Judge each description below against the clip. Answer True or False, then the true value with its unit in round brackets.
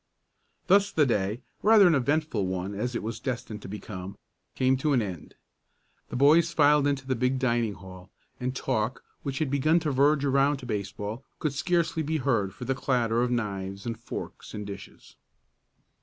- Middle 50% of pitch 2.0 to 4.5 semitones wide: False (5.4 semitones)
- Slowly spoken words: False (180 wpm)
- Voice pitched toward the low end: True (125 Hz)